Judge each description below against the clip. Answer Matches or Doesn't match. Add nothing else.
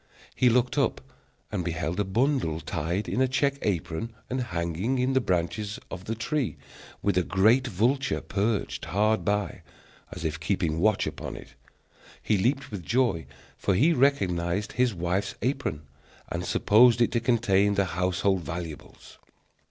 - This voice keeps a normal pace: Matches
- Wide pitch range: Matches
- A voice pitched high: Doesn't match